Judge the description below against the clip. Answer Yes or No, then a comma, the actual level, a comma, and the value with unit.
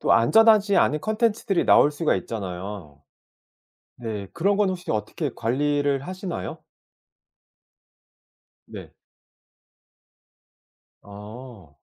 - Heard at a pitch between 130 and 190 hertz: Yes, medium, 140 Hz